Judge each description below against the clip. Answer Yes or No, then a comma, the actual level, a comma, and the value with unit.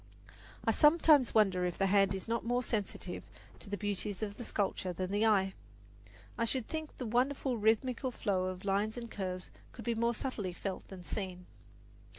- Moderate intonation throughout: Yes, average, 3.8 semitones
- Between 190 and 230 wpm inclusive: No, average, 175 wpm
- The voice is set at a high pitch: Yes, high, 210 Hz